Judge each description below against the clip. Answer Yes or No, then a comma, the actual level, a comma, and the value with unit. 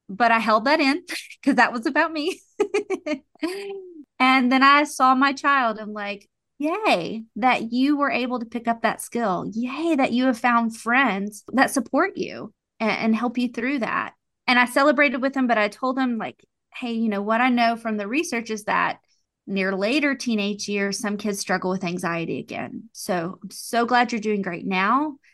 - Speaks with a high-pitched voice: Yes, high, 245 Hz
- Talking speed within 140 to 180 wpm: No, average, 195 wpm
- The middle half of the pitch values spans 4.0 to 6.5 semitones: Yes, average, 4.4 semitones